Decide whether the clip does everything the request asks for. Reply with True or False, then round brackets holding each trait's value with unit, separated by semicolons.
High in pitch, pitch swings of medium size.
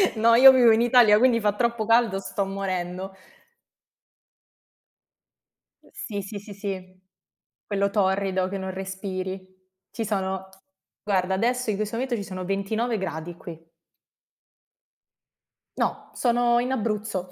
True (200 Hz; 3.3 semitones)